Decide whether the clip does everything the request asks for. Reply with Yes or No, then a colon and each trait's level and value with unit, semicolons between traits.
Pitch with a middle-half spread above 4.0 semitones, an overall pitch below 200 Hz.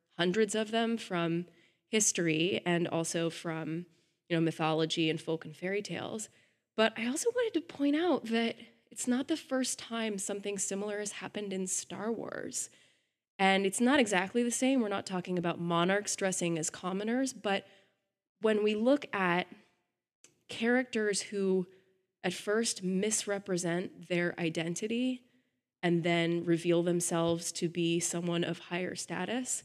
Yes: average, 4.6 semitones; high, 190 Hz